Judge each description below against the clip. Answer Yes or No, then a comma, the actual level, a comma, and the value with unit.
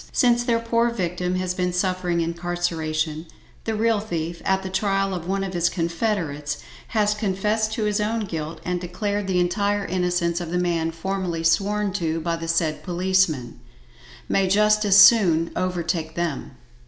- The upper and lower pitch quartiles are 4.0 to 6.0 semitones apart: No, average, 3.4 semitones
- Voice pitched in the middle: Yes, medium, 180 Hz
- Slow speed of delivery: No, average, 160 wpm